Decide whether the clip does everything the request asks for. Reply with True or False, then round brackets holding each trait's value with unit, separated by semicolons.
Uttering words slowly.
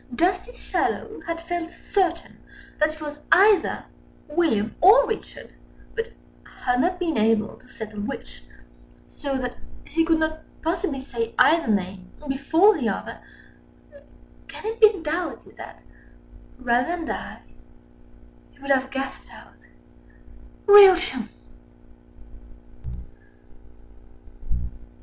True (110 wpm)